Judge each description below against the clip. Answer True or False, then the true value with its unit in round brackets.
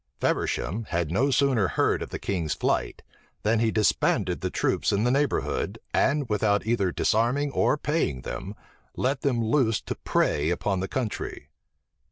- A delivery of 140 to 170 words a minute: True (160 wpm)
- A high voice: False (110 Hz)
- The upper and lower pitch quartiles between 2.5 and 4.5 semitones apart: False (5.3 semitones)